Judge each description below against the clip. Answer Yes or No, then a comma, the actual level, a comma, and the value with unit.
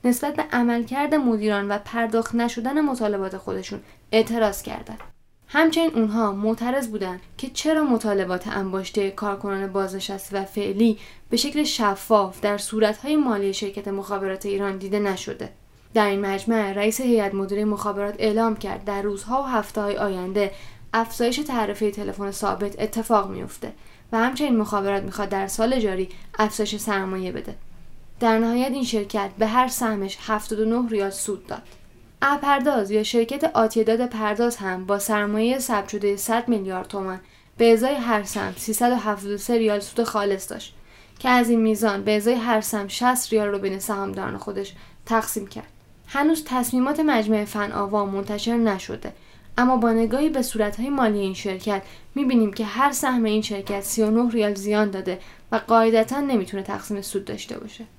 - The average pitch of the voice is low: No, high, 215 Hz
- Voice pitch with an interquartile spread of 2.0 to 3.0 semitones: Yes, average, 2.7 semitones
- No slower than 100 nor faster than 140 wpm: No, average, 150 wpm